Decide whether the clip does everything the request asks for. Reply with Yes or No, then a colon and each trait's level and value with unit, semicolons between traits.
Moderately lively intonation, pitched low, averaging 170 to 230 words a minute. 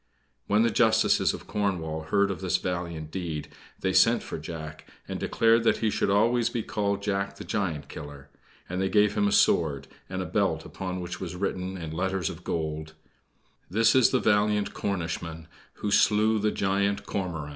Yes: average, 4.1 semitones; very low, 95 Hz; average, 180 wpm